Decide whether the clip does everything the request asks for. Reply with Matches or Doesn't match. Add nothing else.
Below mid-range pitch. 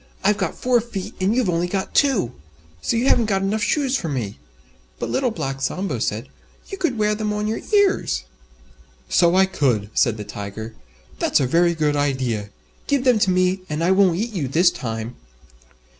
Doesn't match